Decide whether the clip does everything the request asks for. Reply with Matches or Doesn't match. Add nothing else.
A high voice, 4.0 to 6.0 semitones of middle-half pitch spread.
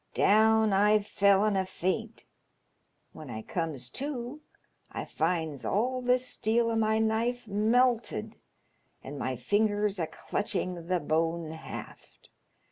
Matches